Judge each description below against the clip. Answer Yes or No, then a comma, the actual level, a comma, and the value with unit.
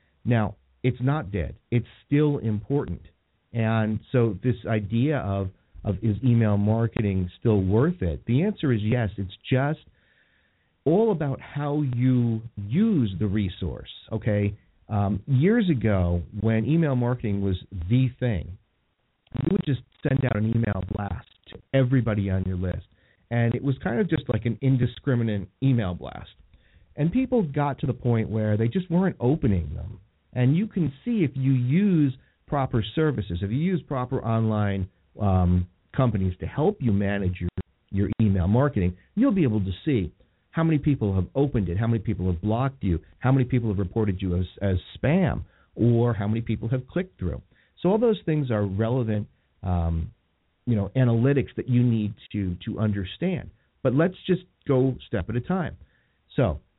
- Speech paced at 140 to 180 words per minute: Yes, average, 170 wpm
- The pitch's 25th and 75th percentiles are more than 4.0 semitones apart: Yes, average, 5.3 semitones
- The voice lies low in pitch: Yes, low, 115 Hz